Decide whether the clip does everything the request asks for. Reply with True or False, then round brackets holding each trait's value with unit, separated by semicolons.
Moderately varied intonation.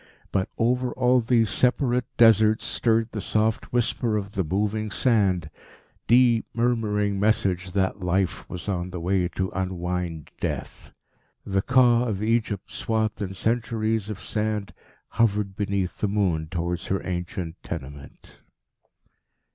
True (3.5 semitones)